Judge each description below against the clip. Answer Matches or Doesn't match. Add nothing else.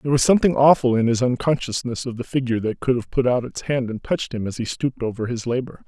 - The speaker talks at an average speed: Doesn't match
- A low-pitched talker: Matches